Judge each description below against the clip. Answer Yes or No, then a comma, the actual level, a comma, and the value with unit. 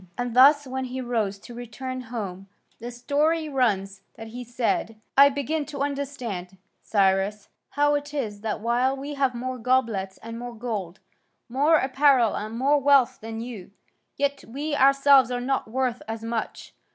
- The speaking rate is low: No, average, 165 wpm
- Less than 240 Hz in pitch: No, high, 245 Hz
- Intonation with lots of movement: No, average, 3.7 semitones